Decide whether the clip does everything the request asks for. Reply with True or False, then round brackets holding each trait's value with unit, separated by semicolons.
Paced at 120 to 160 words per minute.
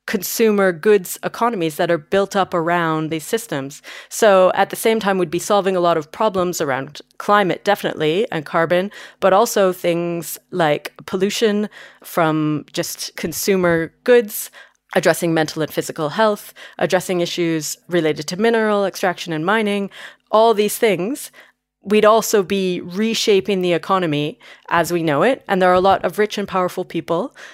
True (155 wpm)